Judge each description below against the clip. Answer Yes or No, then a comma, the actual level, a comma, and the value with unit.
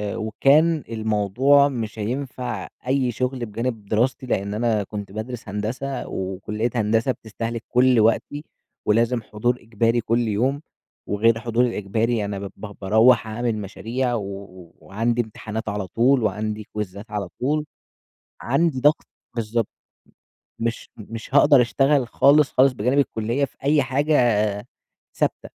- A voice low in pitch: Yes, low, 115 Hz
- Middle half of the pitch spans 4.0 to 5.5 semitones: No, average, 3.3 semitones